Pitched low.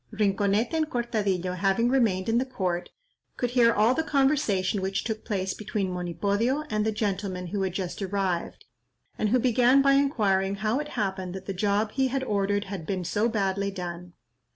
No: high, 205 Hz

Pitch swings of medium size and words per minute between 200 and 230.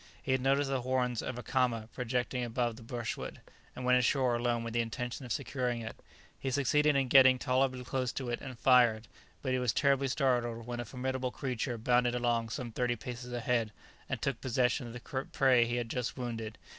No: narrow, 1.6 semitones; fast, 205 wpm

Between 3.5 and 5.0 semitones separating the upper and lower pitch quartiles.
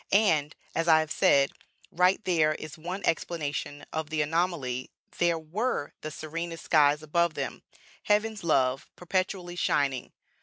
No: average, 2.9 semitones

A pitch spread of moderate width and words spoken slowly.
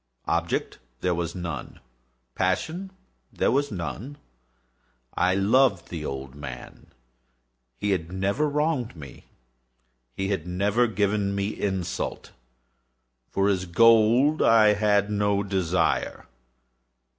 Yes: average, 4.1 semitones; slow, 110 wpm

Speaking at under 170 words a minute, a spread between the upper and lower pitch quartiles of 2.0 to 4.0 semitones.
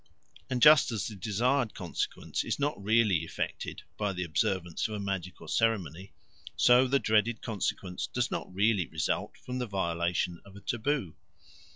No: average, 160 wpm; average, 4.5 semitones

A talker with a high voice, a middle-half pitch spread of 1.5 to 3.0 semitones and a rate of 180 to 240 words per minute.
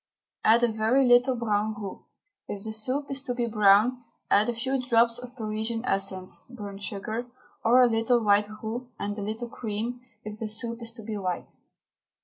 Yes: high, 225 Hz; narrow, 2.6 semitones; average, 185 wpm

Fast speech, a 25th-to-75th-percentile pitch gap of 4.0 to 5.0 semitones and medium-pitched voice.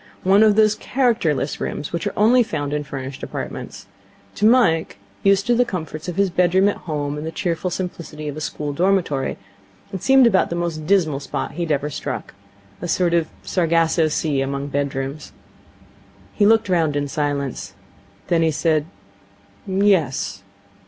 No: average, 165 wpm; average, 4.7 semitones; medium, 165 Hz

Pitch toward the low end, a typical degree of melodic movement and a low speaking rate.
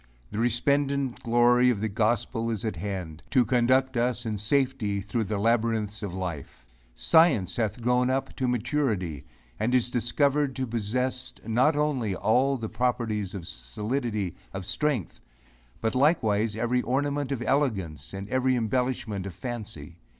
No: low, 120 Hz; average, 4.0 semitones; average, 150 wpm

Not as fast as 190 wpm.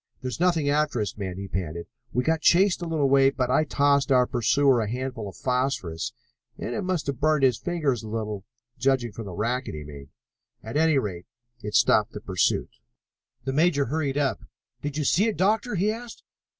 No: average, 200 wpm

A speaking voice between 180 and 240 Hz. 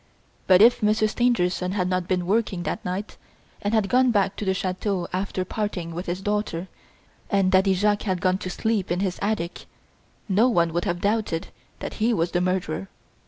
Yes: high, 190 Hz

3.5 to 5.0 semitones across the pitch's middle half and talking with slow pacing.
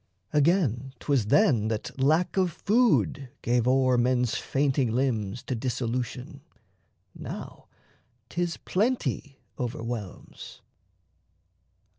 Yes: average, 3.9 semitones; slow, 90 wpm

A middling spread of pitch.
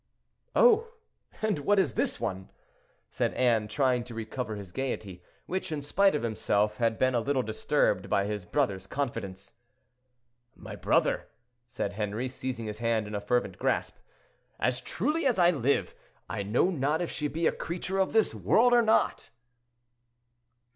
No: wide, 7.5 semitones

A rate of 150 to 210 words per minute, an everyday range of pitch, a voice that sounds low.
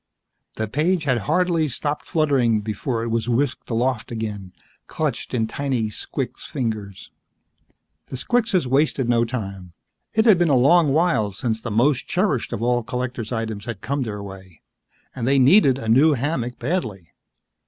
Yes: average, 160 wpm; average, 4.7 semitones; low, 125 Hz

